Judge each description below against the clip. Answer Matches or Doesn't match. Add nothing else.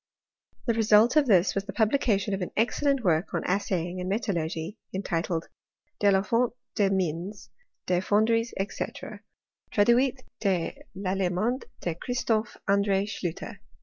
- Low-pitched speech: Doesn't match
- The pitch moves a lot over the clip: Doesn't match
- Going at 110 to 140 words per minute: Matches